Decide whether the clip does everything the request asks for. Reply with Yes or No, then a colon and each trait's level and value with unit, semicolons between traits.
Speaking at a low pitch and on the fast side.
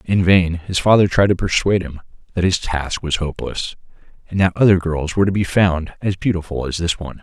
Yes: very low, 90 Hz; fast, 215 wpm